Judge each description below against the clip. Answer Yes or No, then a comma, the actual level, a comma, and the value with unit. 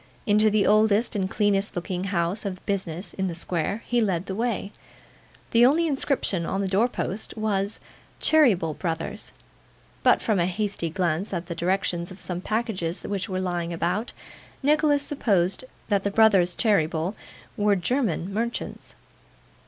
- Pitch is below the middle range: No, high, 195 Hz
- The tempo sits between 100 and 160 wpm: Yes, average, 150 wpm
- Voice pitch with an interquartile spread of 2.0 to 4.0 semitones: Yes, average, 3.6 semitones